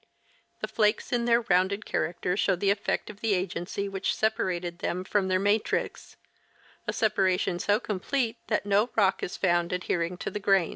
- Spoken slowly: No, average, 175 wpm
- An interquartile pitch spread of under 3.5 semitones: Yes, average, 2.7 semitones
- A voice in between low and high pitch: No, high, 195 Hz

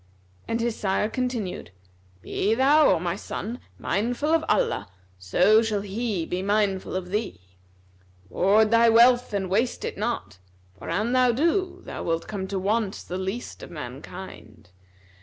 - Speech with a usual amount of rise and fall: Yes, average, 4.1 semitones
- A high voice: Yes, high, 210 Hz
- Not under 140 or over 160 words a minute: Yes, average, 155 wpm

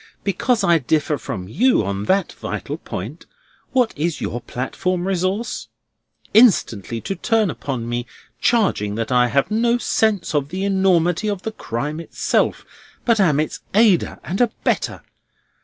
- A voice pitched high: No, medium, 175 Hz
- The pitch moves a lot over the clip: Yes, wide, 8.0 semitones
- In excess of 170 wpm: No, average, 145 wpm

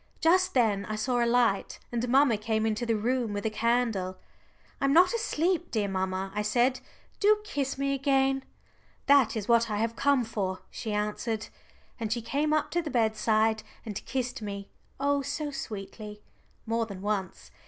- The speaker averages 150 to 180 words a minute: Yes, average, 175 wpm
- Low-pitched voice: No, high, 230 Hz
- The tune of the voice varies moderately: Yes, average, 4.4 semitones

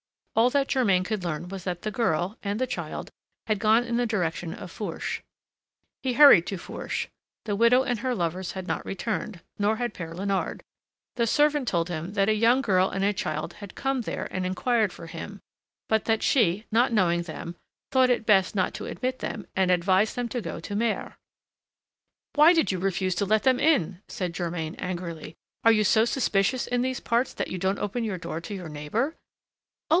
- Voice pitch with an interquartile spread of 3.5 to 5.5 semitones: Yes, average, 4.7 semitones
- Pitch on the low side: No, high, 205 Hz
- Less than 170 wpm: No, average, 200 wpm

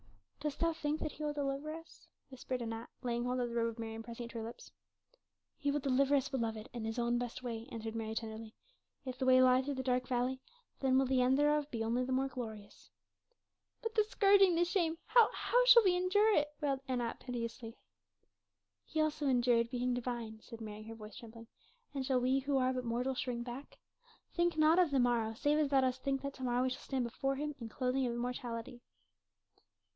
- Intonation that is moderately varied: Yes, average, 3.3 semitones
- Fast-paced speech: Yes, fast, 215 wpm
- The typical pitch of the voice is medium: No, very high, 255 Hz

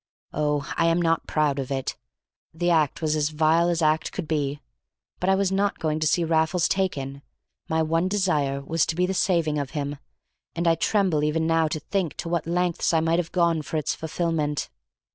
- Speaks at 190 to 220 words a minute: Yes, fast, 205 wpm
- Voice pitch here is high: No, medium, 160 Hz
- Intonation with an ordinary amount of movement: No, narrow, 2.3 semitones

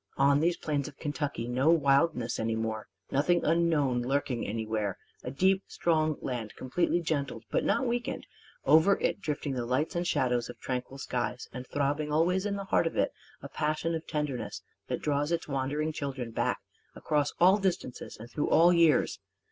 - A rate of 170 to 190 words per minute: Yes, average, 175 wpm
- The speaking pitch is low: No, medium, 145 Hz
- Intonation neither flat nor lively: Yes, average, 4.7 semitones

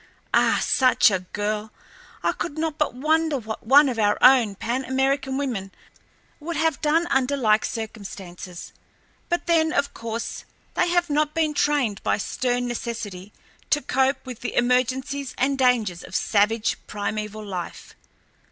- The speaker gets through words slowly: No, average, 150 wpm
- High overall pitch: Yes, very high, 255 Hz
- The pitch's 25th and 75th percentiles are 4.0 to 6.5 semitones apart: Yes, average, 5.1 semitones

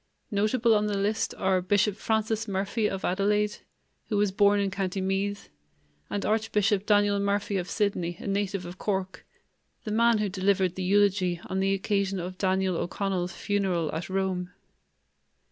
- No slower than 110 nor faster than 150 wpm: No, average, 160 wpm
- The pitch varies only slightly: Yes, narrow, 1.7 semitones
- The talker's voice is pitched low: No, high, 200 Hz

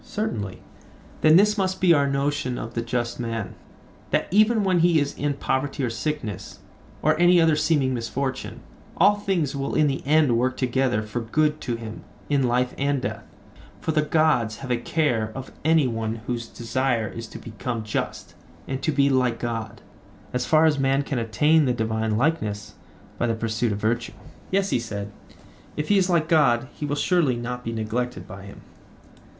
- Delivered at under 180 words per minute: No, average, 185 wpm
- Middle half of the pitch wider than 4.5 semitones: Yes, average, 5.0 semitones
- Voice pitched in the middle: No, low, 130 Hz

